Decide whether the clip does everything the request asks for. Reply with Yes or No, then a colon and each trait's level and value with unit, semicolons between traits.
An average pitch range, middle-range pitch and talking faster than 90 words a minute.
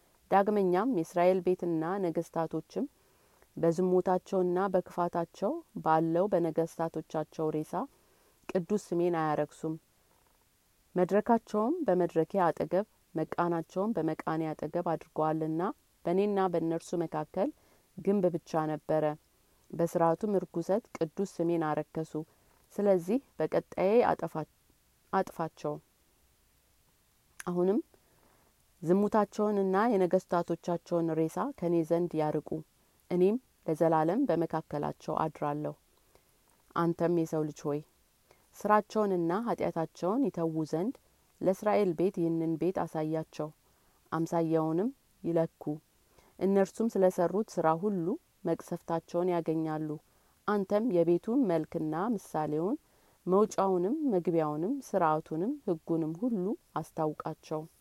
No: average, 3.1 semitones; medium, 170 Hz; average, 80 wpm